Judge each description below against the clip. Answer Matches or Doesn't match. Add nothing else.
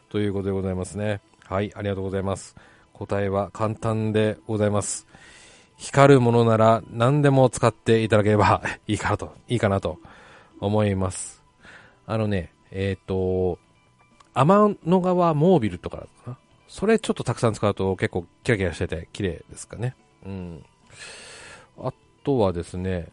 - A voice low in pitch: Matches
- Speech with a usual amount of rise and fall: Matches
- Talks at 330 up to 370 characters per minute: Doesn't match